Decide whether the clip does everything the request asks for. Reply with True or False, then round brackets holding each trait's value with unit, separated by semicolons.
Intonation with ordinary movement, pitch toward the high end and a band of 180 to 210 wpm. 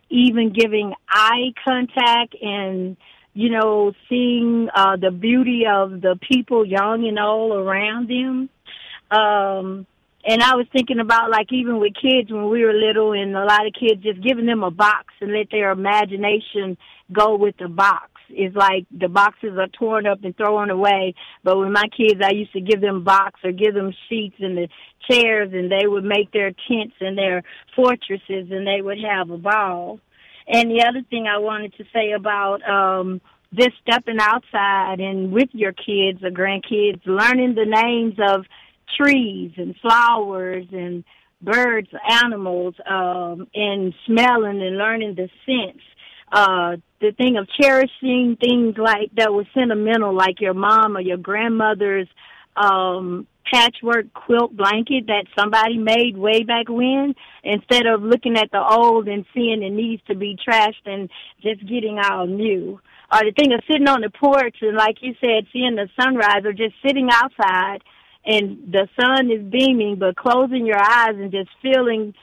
False (3.2 semitones; 210 Hz; 170 wpm)